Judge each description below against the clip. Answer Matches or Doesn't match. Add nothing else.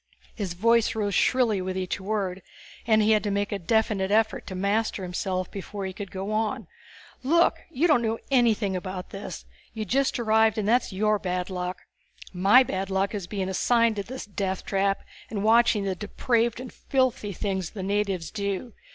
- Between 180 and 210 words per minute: Matches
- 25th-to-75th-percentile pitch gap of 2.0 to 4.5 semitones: Matches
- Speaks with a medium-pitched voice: Doesn't match